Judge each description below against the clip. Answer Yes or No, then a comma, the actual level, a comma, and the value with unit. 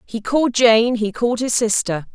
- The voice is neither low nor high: No, high, 230 Hz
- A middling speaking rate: Yes, average, 195 wpm